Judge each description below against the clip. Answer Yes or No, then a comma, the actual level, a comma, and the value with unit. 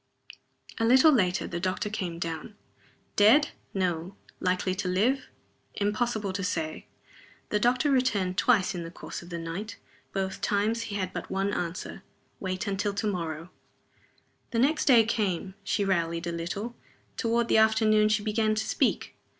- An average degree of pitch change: Yes, average, 3.5 semitones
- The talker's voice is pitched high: Yes, high, 200 Hz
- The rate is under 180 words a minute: Yes, average, 160 wpm